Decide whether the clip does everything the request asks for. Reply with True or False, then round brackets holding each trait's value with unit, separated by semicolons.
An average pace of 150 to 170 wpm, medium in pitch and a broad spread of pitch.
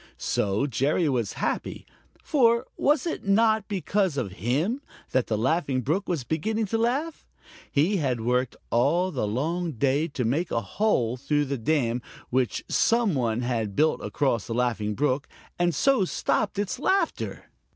True (160 wpm; 145 Hz; 8.3 semitones)